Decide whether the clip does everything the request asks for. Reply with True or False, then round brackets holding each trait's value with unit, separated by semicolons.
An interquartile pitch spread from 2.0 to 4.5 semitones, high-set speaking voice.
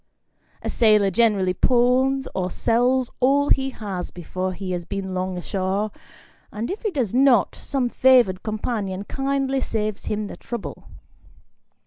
False (5.4 semitones; 220 Hz)